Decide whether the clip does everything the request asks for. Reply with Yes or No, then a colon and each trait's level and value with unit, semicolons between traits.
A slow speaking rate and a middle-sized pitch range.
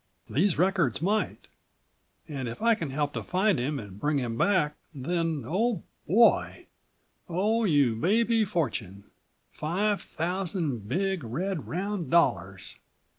No: slow, 125 wpm; wide, 6.3 semitones